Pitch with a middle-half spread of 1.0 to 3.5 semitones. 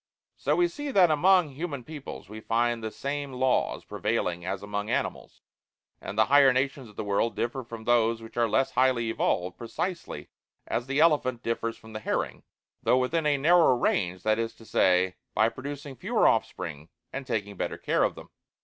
No: average, 4.5 semitones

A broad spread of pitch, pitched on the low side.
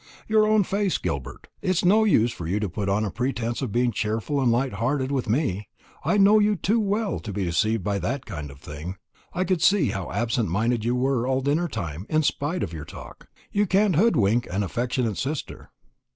Yes: wide, 9.0 semitones; low, 125 Hz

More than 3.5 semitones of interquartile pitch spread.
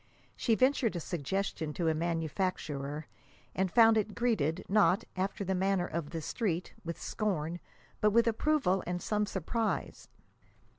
Yes: average, 4.5 semitones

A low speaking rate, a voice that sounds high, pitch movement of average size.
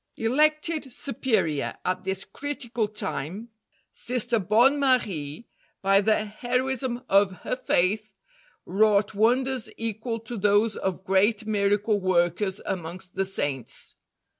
Yes: slow, 115 wpm; high, 215 Hz; average, 4.0 semitones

